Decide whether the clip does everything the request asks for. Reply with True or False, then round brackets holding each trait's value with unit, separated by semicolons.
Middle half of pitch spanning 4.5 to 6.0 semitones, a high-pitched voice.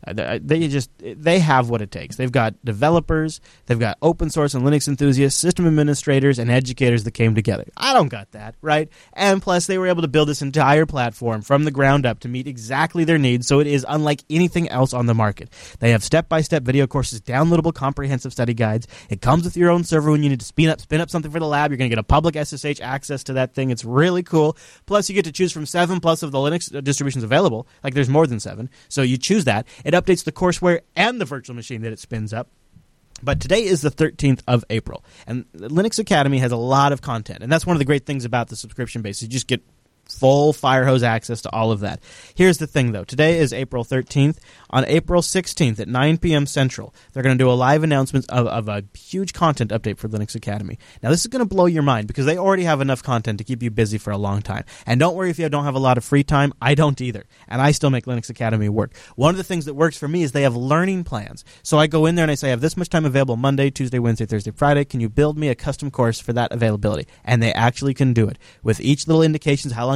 False (4.8 semitones; 140 Hz)